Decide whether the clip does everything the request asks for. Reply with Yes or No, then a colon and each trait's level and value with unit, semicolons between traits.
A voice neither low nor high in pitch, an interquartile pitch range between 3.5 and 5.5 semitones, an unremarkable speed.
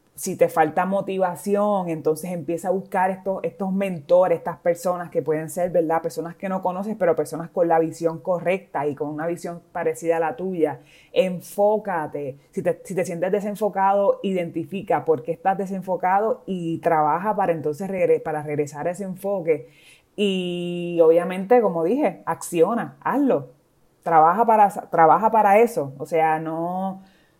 No: medium, 175 Hz; average, 2.9 semitones; average, 155 wpm